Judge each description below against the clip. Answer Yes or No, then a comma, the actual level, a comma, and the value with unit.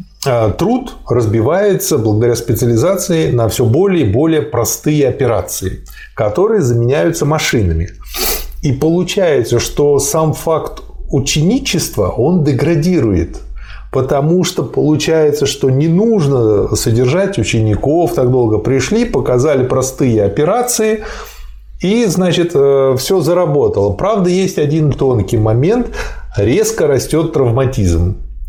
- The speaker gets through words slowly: Yes, slow, 100 wpm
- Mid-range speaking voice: Yes, medium, 145 Hz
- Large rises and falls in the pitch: Yes, wide, 6.8 semitones